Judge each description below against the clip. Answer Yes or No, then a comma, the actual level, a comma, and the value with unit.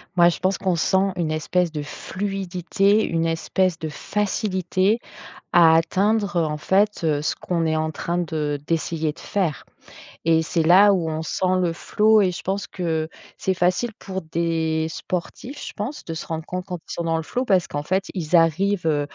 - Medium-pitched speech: Yes, medium, 175 Hz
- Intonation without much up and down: No, average, 3.0 semitones